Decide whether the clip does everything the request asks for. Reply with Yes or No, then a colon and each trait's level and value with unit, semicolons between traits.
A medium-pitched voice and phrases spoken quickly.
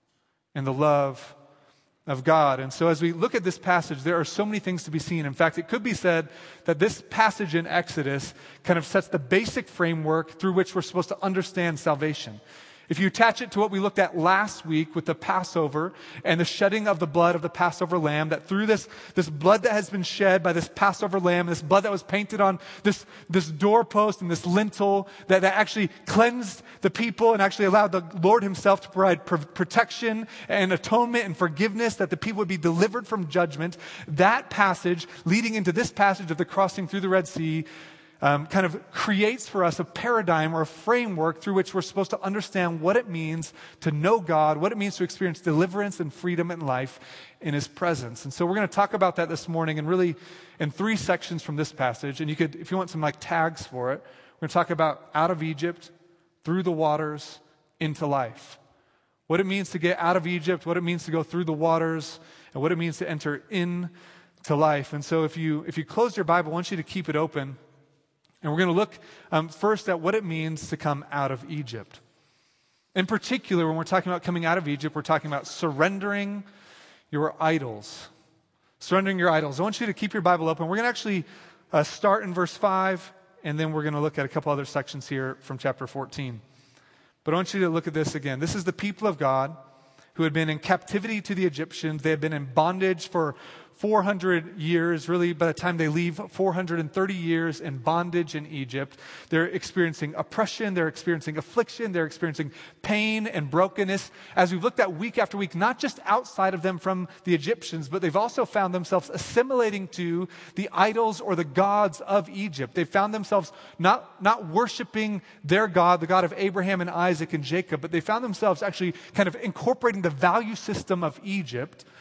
Yes: medium, 175 Hz; fast, 210 wpm